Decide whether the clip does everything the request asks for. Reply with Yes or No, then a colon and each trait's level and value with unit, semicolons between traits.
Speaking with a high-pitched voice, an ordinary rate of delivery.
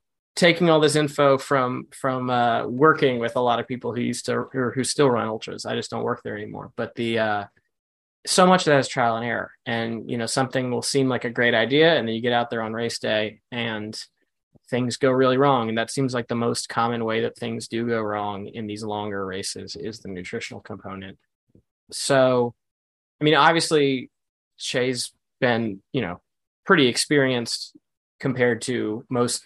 No: low, 120 Hz; average, 195 wpm